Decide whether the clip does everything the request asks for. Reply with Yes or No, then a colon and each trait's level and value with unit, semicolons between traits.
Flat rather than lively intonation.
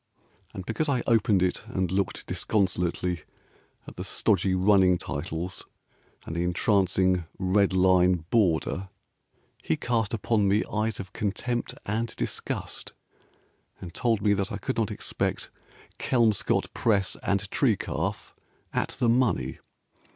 No: average, 3.4 semitones